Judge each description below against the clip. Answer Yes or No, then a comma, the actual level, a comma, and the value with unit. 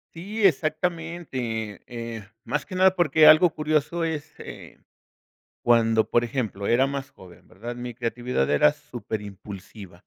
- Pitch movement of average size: No, wide, 6.0 semitones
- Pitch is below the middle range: Yes, low, 125 Hz